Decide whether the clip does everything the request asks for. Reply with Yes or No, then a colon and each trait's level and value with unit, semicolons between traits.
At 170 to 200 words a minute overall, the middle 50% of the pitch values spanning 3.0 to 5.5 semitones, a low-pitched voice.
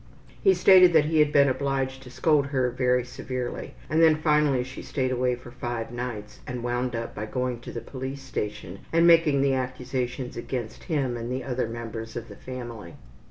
No: average, 195 wpm; narrow, 2.6 semitones; low, 125 Hz